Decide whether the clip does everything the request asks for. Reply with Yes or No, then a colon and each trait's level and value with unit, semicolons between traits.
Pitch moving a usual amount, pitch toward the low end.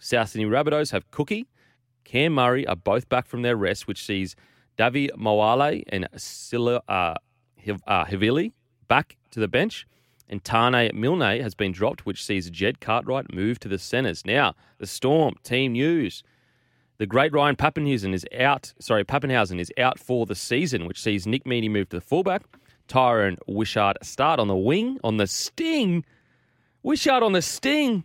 No: wide, 5.9 semitones; low, 120 Hz